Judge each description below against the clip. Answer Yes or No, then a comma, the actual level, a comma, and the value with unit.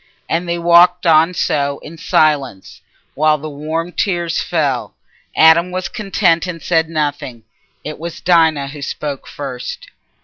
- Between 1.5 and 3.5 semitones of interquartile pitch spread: Yes, narrow, 2.6 semitones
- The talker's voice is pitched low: No, medium, 160 Hz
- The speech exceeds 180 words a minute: No, average, 140 wpm